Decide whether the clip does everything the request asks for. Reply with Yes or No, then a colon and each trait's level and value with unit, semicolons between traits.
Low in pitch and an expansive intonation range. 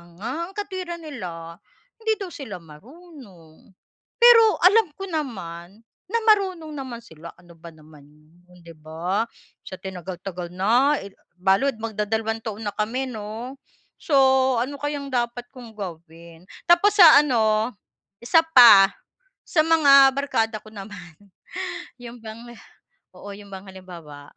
No: high, 225 Hz; wide, 8.0 semitones